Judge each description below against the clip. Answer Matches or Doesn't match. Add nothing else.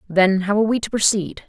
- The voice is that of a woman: Matches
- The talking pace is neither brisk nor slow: Doesn't match